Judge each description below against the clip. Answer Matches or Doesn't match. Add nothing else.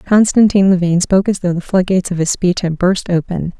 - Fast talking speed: Matches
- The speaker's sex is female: Matches